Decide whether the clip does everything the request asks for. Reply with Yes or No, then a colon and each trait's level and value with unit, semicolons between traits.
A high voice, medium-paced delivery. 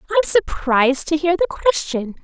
Yes: very high, 315 Hz; average, 160 wpm